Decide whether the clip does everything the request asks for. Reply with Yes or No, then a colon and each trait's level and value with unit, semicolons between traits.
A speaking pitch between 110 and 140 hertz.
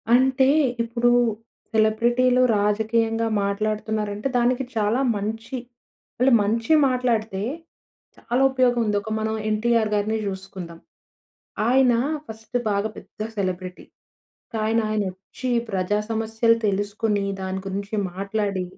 No: high, 220 Hz